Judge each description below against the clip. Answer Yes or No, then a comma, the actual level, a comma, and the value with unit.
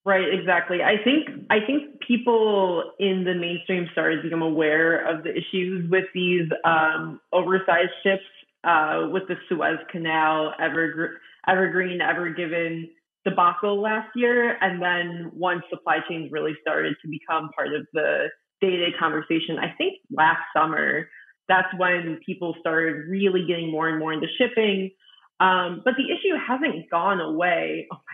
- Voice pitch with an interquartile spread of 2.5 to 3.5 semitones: Yes, average, 3.0 semitones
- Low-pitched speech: No, medium, 180 Hz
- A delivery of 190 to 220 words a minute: No, average, 160 wpm